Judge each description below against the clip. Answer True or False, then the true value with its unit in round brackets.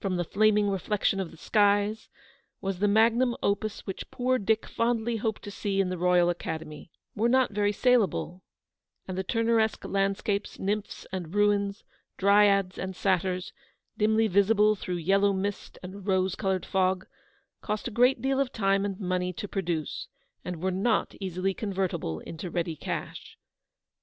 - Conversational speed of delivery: True (160 wpm)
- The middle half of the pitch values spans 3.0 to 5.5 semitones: False (2.6 semitones)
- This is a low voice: False (200 Hz)